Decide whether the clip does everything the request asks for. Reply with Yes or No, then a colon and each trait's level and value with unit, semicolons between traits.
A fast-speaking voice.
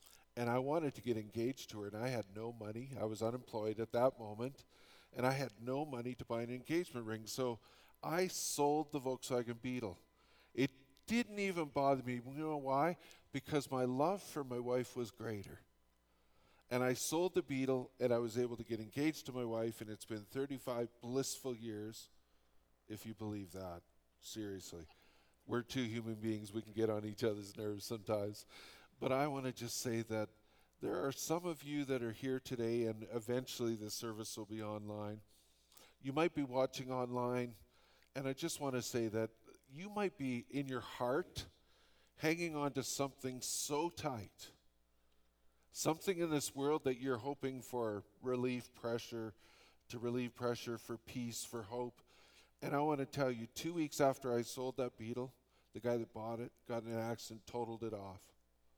No: average, 180 wpm